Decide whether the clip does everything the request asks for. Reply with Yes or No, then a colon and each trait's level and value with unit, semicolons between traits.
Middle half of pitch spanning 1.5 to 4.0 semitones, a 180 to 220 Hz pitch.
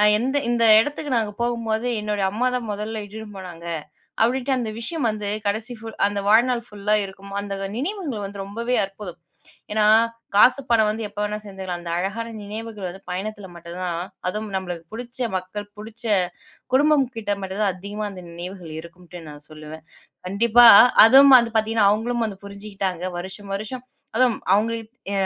Yes: average, 3.2 semitones; high, 210 Hz